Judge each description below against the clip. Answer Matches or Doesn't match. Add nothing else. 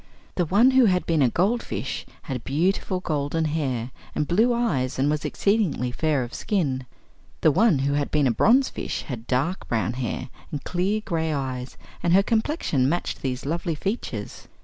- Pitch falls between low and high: Matches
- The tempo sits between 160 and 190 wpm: Matches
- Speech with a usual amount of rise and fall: Doesn't match